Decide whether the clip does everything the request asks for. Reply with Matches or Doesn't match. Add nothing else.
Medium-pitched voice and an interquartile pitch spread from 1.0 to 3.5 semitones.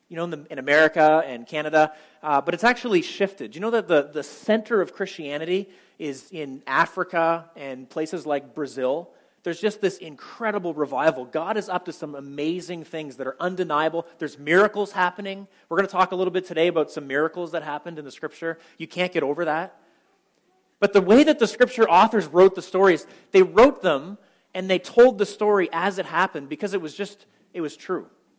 Doesn't match